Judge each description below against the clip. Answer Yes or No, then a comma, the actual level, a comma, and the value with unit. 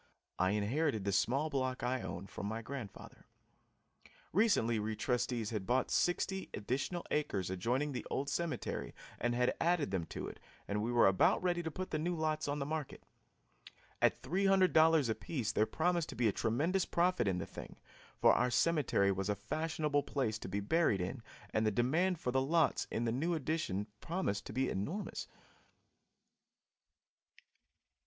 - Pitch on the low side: Yes, low, 130 Hz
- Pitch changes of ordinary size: No, wide, 7.0 semitones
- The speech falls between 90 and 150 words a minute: No, average, 170 wpm